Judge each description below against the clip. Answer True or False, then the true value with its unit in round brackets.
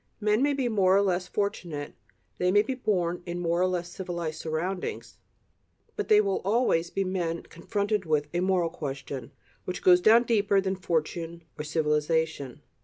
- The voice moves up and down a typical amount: True (3.5 semitones)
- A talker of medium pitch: True (180 Hz)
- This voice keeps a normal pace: True (170 wpm)